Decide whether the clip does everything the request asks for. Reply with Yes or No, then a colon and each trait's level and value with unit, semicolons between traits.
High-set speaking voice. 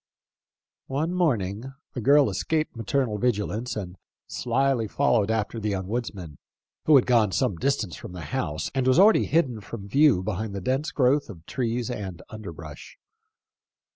No: low, 115 Hz